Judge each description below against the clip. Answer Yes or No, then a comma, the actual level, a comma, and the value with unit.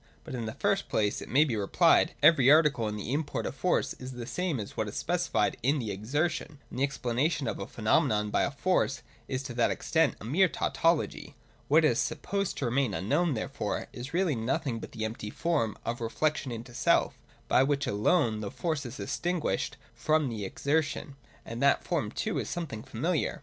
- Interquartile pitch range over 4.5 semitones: Yes, average, 5.3 semitones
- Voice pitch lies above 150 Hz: No, low, 135 Hz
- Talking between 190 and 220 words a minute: Yes, average, 200 wpm